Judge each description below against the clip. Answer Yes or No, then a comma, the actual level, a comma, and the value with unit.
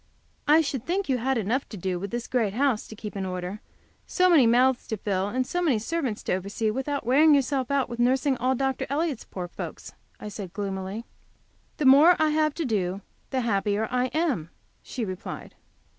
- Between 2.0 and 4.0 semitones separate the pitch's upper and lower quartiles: No, wide, 5.5 semitones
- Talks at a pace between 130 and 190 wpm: No, average, 200 wpm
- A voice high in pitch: Yes, high, 245 Hz